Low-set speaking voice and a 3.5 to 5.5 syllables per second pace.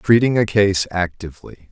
Yes: low, 100 Hz; 5.1 syllables/s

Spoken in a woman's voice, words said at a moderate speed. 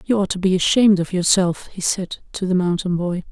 No: female; fast, 235 wpm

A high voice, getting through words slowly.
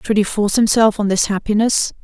No: high, 210 Hz; fast, 205 wpm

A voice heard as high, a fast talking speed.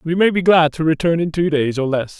No: medium, 160 Hz; fast, 300 wpm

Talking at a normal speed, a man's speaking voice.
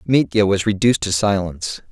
Yes: average, 155 wpm; male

